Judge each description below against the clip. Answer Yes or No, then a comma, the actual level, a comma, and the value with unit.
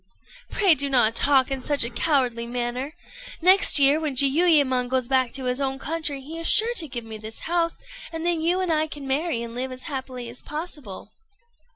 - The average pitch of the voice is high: Yes, very high, 275 Hz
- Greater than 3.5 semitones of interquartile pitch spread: Yes, average, 4.2 semitones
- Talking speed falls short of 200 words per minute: No, fast, 205 wpm